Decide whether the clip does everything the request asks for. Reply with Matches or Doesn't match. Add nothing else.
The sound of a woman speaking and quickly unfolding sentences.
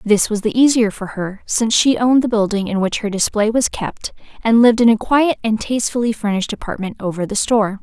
Matches